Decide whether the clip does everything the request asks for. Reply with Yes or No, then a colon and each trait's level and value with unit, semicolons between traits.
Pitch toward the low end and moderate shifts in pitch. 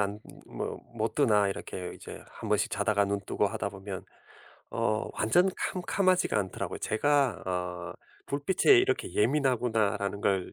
No: low, 110 Hz; wide, 6.1 semitones